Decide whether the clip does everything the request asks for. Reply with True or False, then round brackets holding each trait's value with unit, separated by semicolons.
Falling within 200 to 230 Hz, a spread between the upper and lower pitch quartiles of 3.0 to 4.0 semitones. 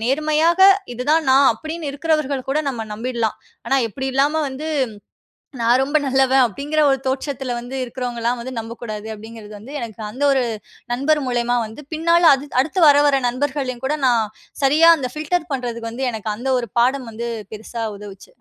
False (260 Hz; 3.7 semitones)